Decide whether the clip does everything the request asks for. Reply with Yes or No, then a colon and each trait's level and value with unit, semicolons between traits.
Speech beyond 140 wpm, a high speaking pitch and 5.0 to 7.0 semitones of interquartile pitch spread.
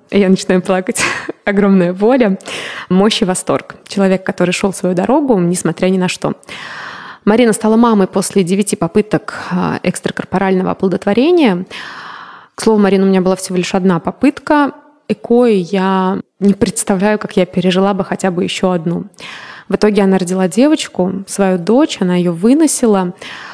No: average, 150 wpm; high, 195 Hz; average, 2.8 semitones